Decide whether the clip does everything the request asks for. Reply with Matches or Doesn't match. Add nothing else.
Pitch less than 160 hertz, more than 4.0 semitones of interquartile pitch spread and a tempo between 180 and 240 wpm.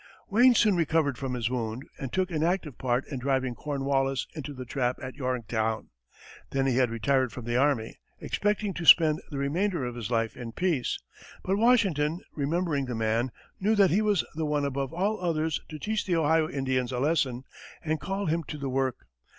Matches